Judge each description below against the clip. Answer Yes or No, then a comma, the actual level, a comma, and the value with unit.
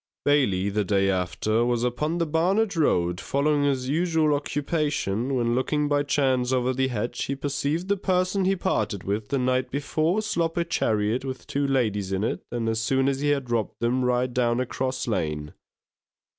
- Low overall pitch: Yes, low, 130 Hz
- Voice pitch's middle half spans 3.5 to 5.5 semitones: Yes, average, 4.2 semitones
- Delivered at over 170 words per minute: Yes, average, 185 wpm